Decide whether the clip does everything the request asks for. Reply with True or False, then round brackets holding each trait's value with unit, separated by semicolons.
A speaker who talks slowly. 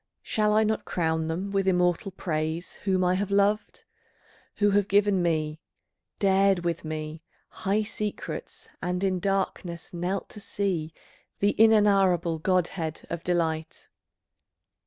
True (130 wpm)